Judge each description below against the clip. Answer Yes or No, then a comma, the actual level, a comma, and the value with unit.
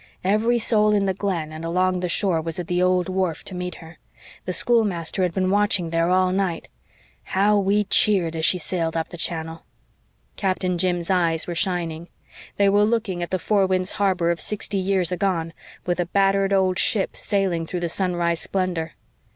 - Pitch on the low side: No, medium, 185 Hz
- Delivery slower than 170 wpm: No, average, 190 wpm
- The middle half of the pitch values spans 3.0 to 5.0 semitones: No, narrow, 2.5 semitones